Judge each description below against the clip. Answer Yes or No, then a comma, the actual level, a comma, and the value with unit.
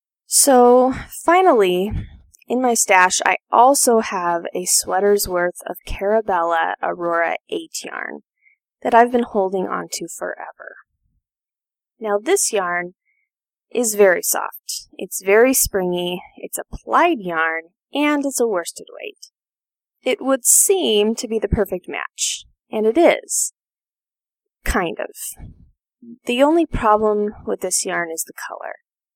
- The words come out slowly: Yes, slow, 125 wpm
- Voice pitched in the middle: No, high, 220 Hz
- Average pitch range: No, wide, 6.8 semitones